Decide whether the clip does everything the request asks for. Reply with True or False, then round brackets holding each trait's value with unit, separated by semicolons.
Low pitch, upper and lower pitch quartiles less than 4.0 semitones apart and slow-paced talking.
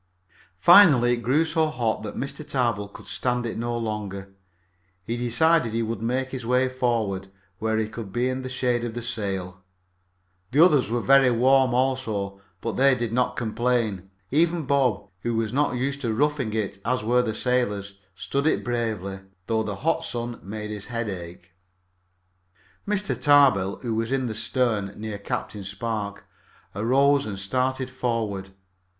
False (120 Hz; 3.5 semitones; 165 wpm)